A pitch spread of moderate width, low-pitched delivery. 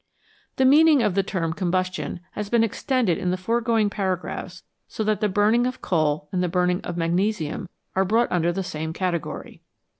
No: average, 3.9 semitones; medium, 185 Hz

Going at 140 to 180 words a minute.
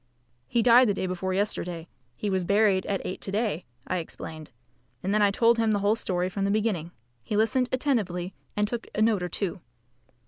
No: fast, 205 wpm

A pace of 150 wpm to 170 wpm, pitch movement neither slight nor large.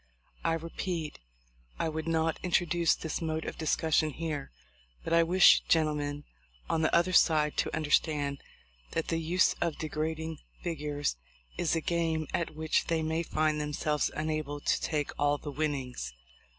No: average, 155 wpm; narrow, 1.7 semitones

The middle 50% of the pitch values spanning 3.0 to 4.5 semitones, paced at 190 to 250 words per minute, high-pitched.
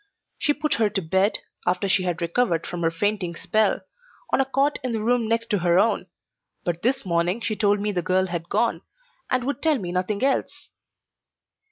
No: average, 5.0 semitones; average, 200 wpm; high, 205 Hz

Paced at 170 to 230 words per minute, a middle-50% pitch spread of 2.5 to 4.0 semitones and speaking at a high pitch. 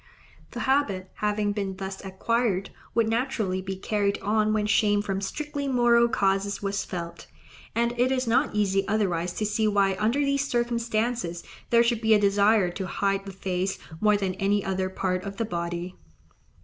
Yes: average, 175 wpm; average, 3.2 semitones; high, 205 Hz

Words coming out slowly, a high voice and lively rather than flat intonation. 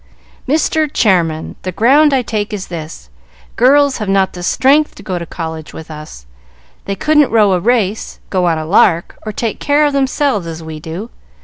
No: average, 190 wpm; high, 200 Hz; wide, 8.0 semitones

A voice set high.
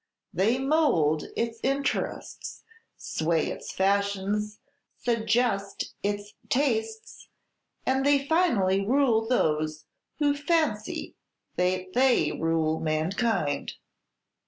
Yes: high, 210 Hz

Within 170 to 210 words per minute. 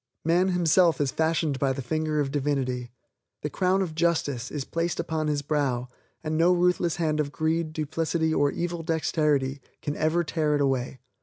Yes: average, 175 wpm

